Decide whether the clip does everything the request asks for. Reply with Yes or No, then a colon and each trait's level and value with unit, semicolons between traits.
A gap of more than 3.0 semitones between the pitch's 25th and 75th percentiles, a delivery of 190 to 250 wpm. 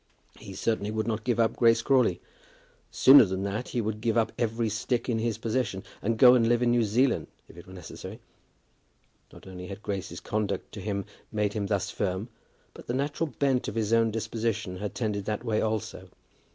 No: narrow, 2.5 semitones; average, 200 wpm